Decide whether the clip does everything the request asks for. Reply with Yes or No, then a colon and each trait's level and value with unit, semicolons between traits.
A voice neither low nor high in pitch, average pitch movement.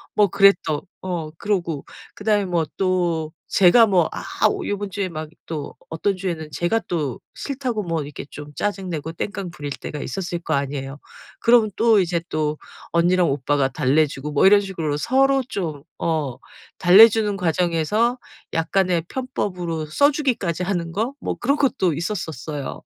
Yes: medium, 175 Hz; average, 4.7 semitones